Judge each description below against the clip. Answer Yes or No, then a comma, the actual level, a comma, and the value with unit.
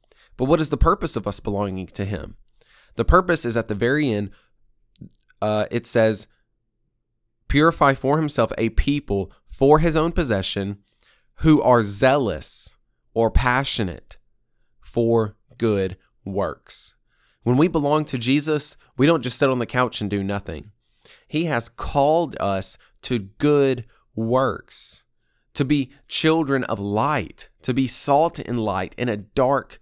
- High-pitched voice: No, low, 120 Hz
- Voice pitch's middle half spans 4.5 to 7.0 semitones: Yes, average, 5.3 semitones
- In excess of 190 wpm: No, average, 145 wpm